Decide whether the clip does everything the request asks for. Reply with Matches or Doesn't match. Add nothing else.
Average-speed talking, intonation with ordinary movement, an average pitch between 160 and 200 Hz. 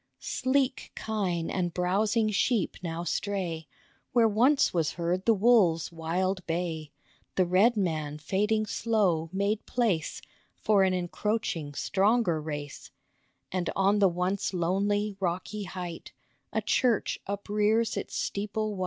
Doesn't match